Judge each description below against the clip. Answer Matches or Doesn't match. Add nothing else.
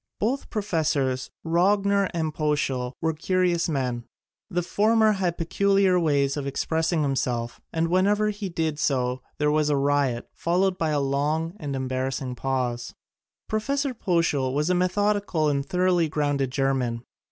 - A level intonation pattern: Doesn't match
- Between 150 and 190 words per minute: Doesn't match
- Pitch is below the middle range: Doesn't match